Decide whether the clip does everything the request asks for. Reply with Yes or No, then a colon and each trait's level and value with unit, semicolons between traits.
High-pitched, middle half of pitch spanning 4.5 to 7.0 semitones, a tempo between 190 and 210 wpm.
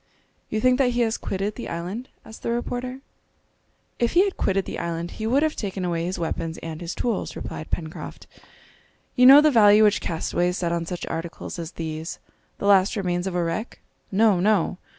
Yes: high, 195 Hz; wide, 5.5 semitones; average, 195 wpm